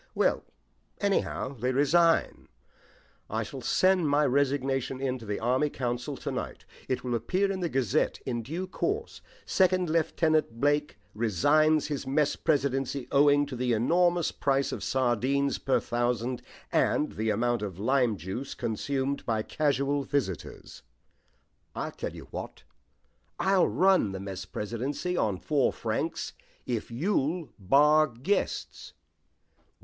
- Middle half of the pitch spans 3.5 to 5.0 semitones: Yes, average, 4.2 semitones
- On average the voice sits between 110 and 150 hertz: Yes, low, 135 Hz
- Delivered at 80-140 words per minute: Yes, slow, 135 wpm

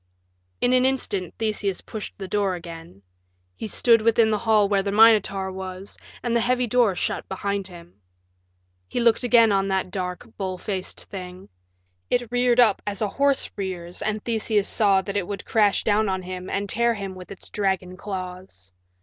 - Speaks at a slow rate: No, average, 180 wpm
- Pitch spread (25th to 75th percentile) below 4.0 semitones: Yes, average, 3.1 semitones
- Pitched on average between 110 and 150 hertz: No, high, 200 Hz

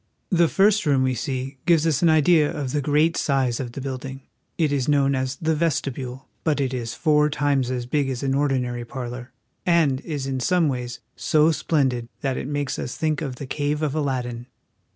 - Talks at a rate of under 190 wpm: No, average, 200 wpm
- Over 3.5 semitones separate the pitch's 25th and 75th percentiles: No, average, 2.9 semitones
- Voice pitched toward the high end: No, medium, 140 Hz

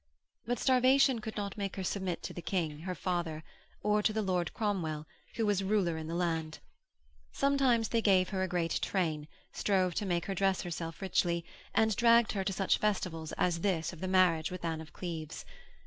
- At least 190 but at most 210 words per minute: Yes, average, 195 wpm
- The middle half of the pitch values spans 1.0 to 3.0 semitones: No, average, 3.8 semitones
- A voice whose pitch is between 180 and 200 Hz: Yes, medium, 185 Hz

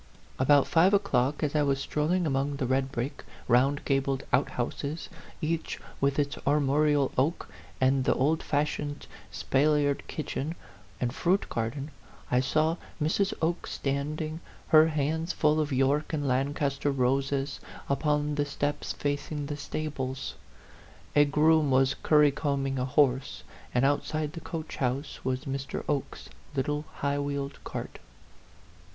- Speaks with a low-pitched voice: No, medium, 145 Hz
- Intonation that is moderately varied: No, narrow, 2.0 semitones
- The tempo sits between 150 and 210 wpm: No, slow, 135 wpm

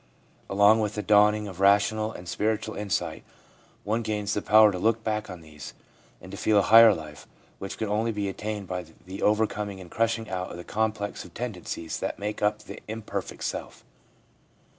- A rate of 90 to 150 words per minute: No, average, 190 wpm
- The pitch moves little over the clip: Yes, narrow, 2.3 semitones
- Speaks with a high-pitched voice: No, low, 105 Hz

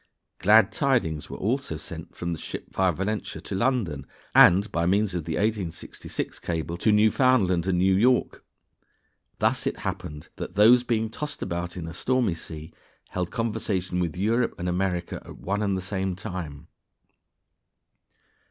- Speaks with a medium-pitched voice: No, very low, 95 Hz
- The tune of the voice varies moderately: Yes, average, 4.1 semitones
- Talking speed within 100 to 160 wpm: Yes, average, 155 wpm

